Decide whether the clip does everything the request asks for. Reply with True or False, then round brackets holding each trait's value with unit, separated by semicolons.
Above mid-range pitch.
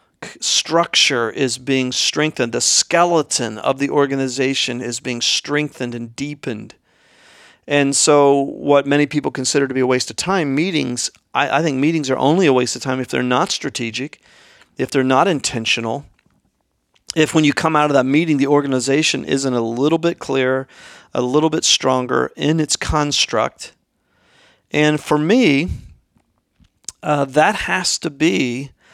False (135 Hz)